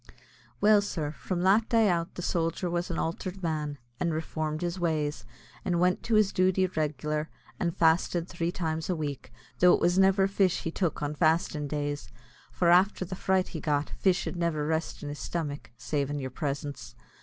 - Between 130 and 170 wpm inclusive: No, average, 190 wpm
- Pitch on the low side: No, medium, 170 Hz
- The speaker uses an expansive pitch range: No, average, 3.3 semitones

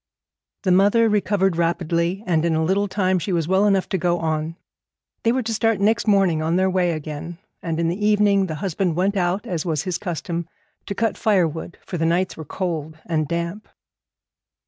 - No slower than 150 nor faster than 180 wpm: No, average, 195 wpm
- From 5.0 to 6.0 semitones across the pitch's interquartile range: No, average, 3.2 semitones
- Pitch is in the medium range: Yes, medium, 180 Hz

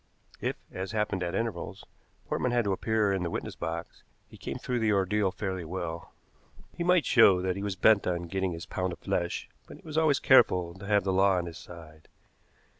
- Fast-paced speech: Yes, fast, 210 wpm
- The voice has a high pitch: No, very low, 95 Hz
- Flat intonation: No, average, 3.5 semitones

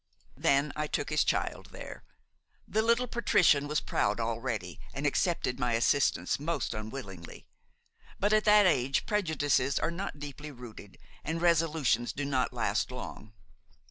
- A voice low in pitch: No, medium, 145 Hz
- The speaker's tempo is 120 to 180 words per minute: Yes, average, 140 wpm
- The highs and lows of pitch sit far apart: Yes, wide, 5.7 semitones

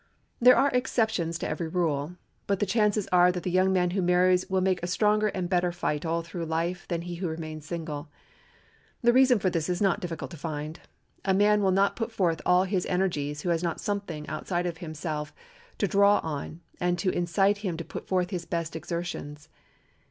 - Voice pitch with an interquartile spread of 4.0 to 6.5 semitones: No, average, 2.7 semitones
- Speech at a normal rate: No, fast, 210 wpm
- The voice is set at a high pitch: No, medium, 180 Hz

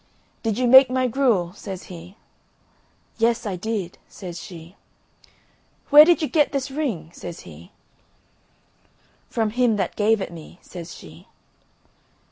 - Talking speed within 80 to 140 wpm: Yes, slow, 135 wpm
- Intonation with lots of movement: Yes, wide, 6.4 semitones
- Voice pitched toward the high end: Yes, high, 210 Hz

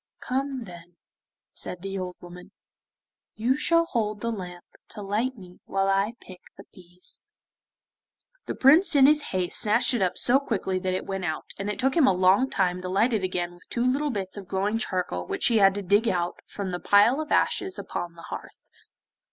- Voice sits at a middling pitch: No, high, 195 Hz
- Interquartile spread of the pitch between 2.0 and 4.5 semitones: No, average, 5.0 semitones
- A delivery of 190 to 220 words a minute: Yes, average, 200 wpm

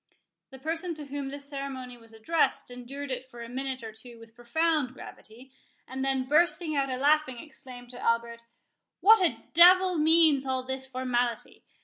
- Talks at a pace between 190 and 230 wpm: No, average, 170 wpm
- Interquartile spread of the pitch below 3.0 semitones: No, average, 3.7 semitones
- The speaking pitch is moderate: No, very high, 265 Hz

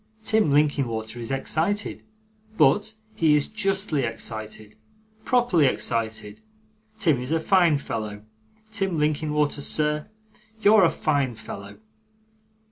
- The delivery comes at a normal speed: No, slow, 110 wpm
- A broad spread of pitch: Yes, wide, 7.4 semitones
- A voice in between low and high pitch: Yes, medium, 150 Hz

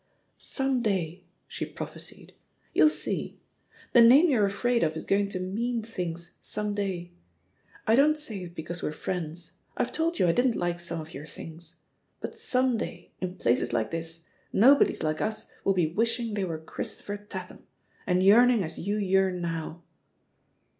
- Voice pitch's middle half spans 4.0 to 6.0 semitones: Yes, wide, 5.5 semitones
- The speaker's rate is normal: Yes, average, 175 wpm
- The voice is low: No, high, 190 Hz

